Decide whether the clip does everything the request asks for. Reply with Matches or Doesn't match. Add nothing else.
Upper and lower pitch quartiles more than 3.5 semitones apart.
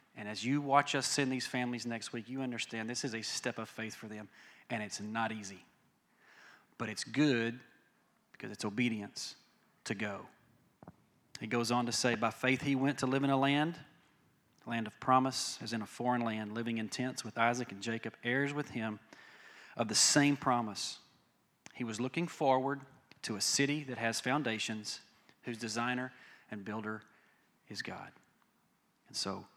Doesn't match